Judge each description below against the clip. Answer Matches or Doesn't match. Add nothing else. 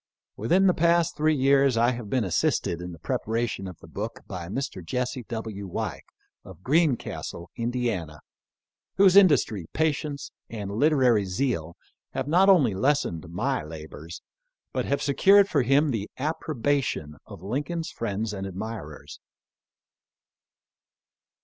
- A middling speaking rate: Doesn't match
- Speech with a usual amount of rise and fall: Doesn't match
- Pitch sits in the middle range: Doesn't match